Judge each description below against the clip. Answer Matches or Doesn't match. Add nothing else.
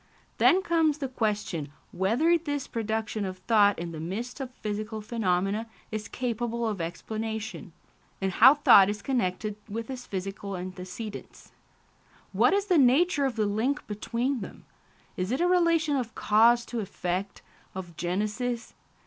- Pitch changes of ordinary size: Matches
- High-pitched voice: Matches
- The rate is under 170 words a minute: Matches